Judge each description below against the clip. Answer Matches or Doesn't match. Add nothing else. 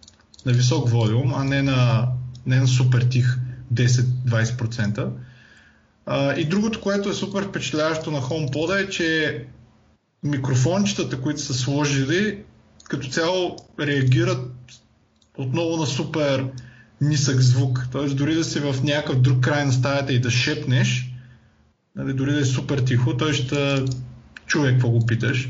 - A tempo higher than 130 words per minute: Matches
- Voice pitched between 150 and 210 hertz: Doesn't match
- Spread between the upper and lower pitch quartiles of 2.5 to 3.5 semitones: Matches